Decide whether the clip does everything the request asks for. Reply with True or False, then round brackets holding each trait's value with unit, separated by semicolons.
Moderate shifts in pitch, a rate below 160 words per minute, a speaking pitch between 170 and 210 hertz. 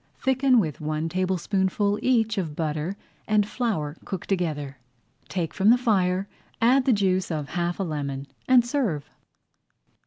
False (6.1 semitones; 145 wpm; 190 Hz)